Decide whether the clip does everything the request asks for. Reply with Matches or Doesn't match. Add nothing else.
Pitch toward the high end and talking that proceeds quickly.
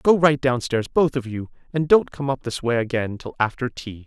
Doesn't match